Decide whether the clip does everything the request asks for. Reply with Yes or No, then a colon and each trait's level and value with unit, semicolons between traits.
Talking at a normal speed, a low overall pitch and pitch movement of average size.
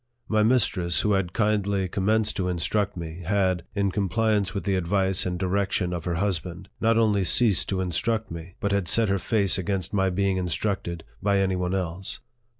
No: average, 180 wpm; very low, 95 Hz; narrow, 2.2 semitones